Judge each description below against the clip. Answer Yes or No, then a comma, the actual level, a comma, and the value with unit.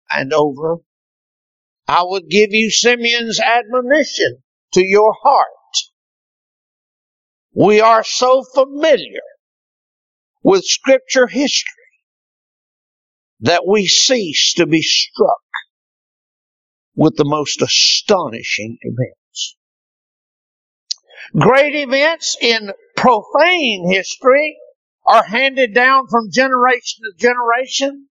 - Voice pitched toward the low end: No, high, 245 Hz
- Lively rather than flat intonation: Yes, wide, 6.1 semitones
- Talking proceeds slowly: Yes, slow, 90 wpm